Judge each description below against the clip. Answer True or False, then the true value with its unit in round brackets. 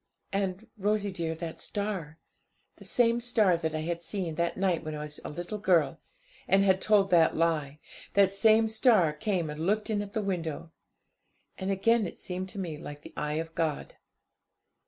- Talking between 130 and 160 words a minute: False (185 wpm)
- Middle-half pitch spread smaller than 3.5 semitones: False (4.1 semitones)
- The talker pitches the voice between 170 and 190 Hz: True (185 Hz)